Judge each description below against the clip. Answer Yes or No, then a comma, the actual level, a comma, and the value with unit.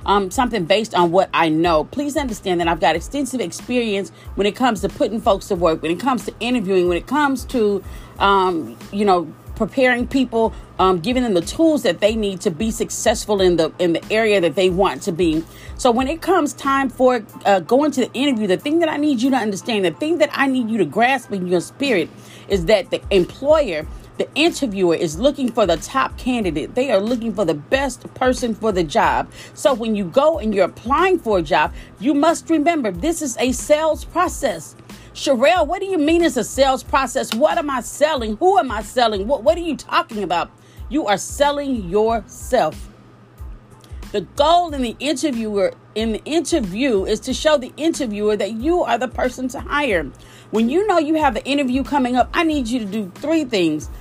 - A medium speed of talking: No, fast, 210 wpm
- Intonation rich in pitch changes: Yes, wide, 6.4 semitones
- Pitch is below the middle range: No, high, 245 Hz